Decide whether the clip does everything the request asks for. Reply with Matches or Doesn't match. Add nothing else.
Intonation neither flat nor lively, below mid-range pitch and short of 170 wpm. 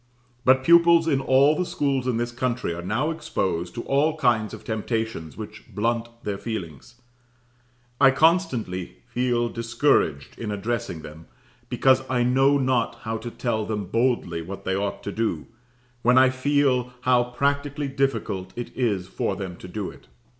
Matches